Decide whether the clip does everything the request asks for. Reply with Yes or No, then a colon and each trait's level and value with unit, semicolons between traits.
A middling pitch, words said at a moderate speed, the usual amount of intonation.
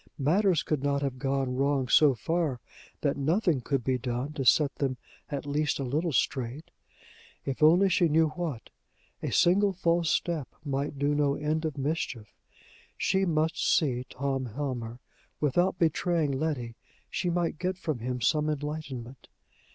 Yes: medium, 145 Hz; average, 155 wpm; average, 3.5 semitones